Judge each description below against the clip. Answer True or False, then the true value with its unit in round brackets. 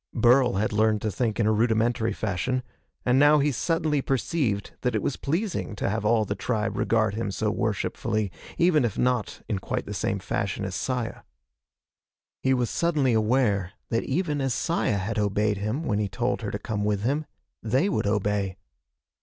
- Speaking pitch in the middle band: False (115 Hz)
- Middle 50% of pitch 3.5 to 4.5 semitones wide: True (4.0 semitones)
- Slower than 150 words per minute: False (185 wpm)